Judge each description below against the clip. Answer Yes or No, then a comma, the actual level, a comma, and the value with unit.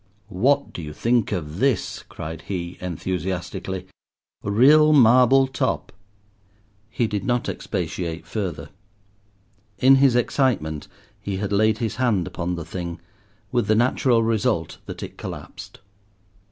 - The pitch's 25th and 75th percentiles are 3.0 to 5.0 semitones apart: No, wide, 5.5 semitones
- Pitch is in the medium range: No, low, 105 Hz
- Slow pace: Yes, slow, 125 wpm